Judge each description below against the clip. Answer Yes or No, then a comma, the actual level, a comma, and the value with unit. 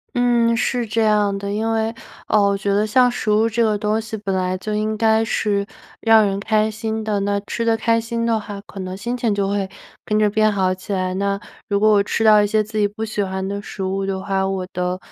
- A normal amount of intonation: No, narrow, 1.9 semitones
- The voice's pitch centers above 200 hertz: Yes, high, 210 Hz